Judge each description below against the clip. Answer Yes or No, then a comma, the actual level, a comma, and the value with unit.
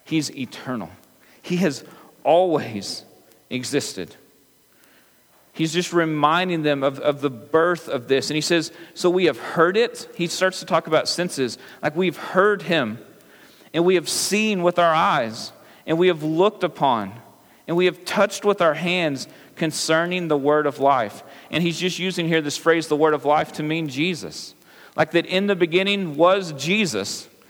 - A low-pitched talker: No, medium, 165 Hz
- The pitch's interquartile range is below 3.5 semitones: Yes, average, 3.1 semitones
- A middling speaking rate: Yes, average, 170 wpm